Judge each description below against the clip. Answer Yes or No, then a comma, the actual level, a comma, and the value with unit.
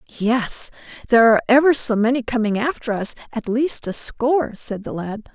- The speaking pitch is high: Yes, high, 235 Hz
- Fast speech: No, average, 180 wpm